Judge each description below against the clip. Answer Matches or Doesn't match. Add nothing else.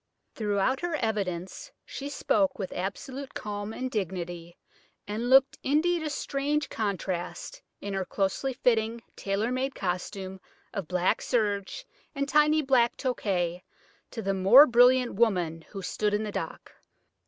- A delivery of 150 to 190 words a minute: Doesn't match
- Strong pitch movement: Matches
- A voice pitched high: Matches